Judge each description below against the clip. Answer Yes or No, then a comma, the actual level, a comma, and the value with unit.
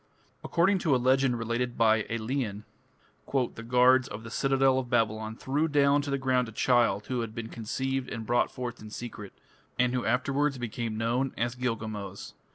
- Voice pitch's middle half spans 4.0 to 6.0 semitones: No, average, 2.8 semitones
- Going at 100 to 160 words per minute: No, average, 175 wpm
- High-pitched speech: No, low, 120 Hz